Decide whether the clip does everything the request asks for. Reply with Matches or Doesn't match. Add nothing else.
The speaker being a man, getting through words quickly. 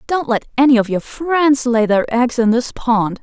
Doesn't match